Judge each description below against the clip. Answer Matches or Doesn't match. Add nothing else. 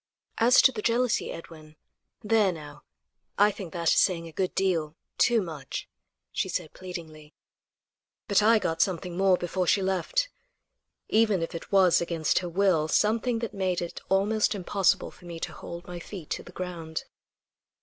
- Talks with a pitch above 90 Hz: Matches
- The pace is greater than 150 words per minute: Matches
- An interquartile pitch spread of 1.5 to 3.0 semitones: Doesn't match